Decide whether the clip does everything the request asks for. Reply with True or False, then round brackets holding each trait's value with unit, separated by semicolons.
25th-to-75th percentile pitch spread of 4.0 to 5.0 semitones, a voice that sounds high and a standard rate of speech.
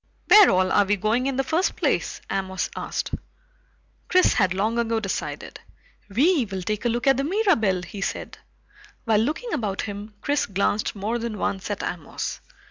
False (5.5 semitones; 220 Hz; 170 wpm)